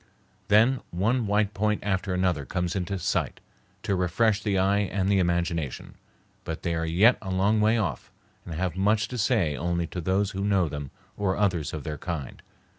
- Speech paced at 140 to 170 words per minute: No, average, 190 wpm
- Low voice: Yes, very low, 95 Hz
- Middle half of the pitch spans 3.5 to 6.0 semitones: No, average, 3.1 semitones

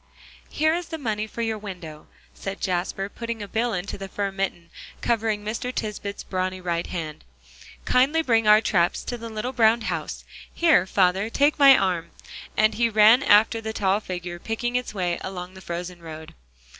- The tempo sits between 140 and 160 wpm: No, average, 180 wpm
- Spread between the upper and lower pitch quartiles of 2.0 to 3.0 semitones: No, average, 3.9 semitones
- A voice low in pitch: No, high, 210 Hz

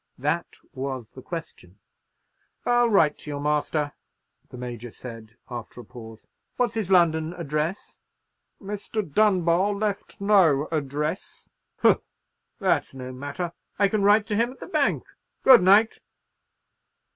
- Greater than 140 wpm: No, slow, 135 wpm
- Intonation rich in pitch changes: Yes, wide, 7.3 semitones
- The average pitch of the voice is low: No, medium, 160 Hz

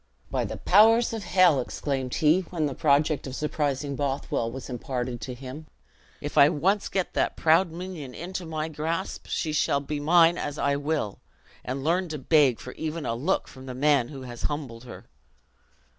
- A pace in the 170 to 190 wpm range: Yes, average, 185 wpm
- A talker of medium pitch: Yes, medium, 150 Hz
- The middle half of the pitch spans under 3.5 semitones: No, average, 3.9 semitones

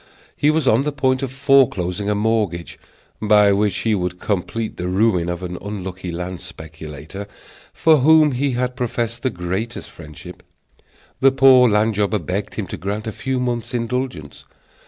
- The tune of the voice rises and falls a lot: Yes, wide, 5.7 semitones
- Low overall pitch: Yes, low, 105 Hz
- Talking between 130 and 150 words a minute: No, average, 165 wpm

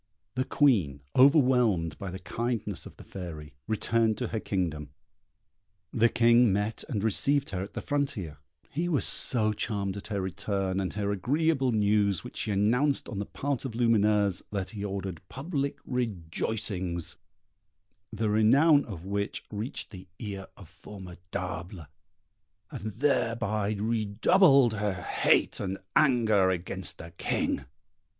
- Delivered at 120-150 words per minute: Yes, average, 140 wpm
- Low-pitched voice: Yes, low, 105 Hz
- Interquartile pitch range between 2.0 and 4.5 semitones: Yes, average, 4.1 semitones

